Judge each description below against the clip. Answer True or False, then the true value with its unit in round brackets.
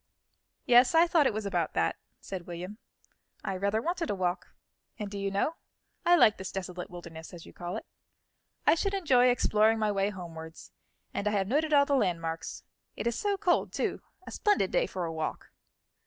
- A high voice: True (205 Hz)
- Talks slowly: False (195 wpm)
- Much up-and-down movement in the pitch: True (8.0 semitones)